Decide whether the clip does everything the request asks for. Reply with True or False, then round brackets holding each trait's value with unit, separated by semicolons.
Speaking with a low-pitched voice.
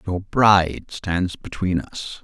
True (90 Hz)